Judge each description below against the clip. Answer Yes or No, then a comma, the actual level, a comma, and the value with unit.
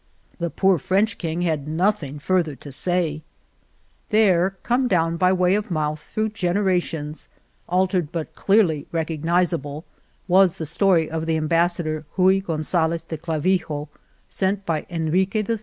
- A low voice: No, medium, 170 Hz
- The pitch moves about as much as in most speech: Yes, average, 3.1 semitones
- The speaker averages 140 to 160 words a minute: Yes, average, 150 wpm